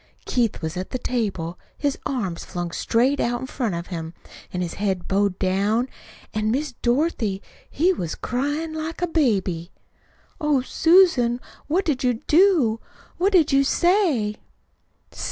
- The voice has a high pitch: Yes, high, 245 Hz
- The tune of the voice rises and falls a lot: Yes, wide, 7.6 semitones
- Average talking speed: Yes, average, 150 wpm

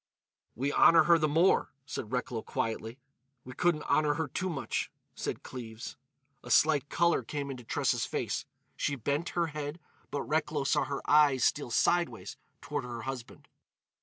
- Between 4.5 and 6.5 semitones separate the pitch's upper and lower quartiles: No, average, 3.7 semitones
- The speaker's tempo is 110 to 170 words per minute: Yes, average, 160 wpm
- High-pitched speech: No, medium, 145 Hz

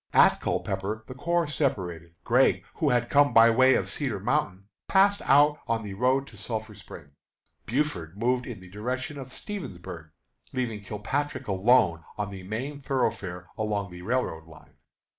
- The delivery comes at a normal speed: Yes, average, 160 wpm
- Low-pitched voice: Yes, low, 115 Hz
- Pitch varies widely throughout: Yes, wide, 5.8 semitones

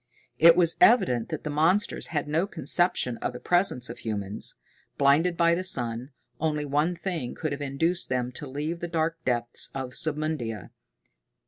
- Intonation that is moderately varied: Yes, average, 5.0 semitones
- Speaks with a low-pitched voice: No, medium, 150 Hz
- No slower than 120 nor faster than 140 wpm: No, average, 165 wpm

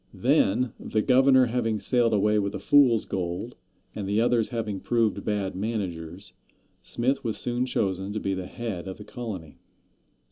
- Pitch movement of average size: Yes, average, 3.7 semitones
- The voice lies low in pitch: Yes, low, 110 Hz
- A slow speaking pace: No, average, 155 wpm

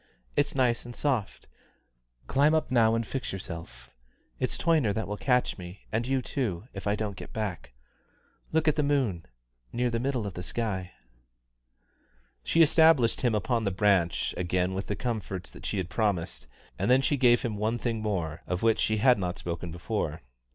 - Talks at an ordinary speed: Yes, average, 185 wpm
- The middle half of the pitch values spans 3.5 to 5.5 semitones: Yes, average, 5.0 semitones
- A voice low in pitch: Yes, low, 110 Hz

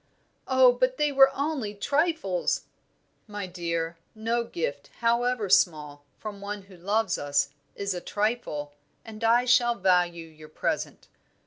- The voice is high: Yes, high, 205 Hz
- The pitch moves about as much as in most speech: No, wide, 6.0 semitones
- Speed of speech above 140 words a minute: No, slow, 135 wpm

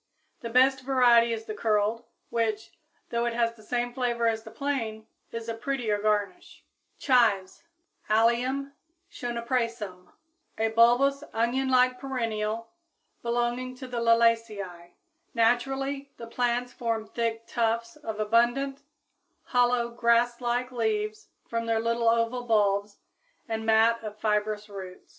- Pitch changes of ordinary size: No, narrow, 1.9 semitones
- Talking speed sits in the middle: No, slow, 130 wpm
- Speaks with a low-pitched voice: No, high, 230 Hz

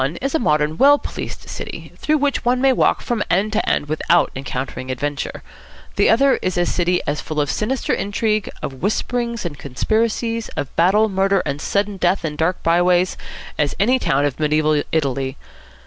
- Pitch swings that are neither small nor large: No, wide, 6.9 semitones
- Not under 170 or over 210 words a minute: Yes, average, 185 wpm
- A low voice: No, medium, 180 Hz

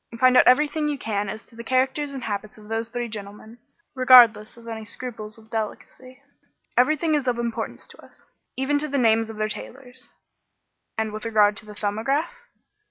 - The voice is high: Yes, high, 235 Hz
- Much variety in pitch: No, average, 3.3 semitones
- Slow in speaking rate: No, average, 185 wpm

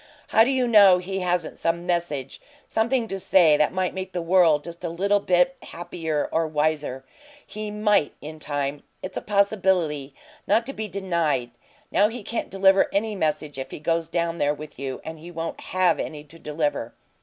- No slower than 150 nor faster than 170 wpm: No, average, 190 wpm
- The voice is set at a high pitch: No, medium, 170 Hz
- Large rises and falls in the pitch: No, average, 4.2 semitones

